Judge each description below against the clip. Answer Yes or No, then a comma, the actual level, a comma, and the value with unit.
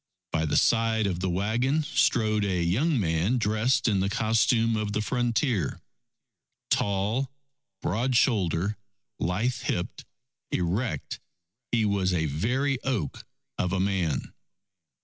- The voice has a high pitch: No, low, 105 Hz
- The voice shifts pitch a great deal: No, average, 4.6 semitones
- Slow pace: Yes, slow, 125 wpm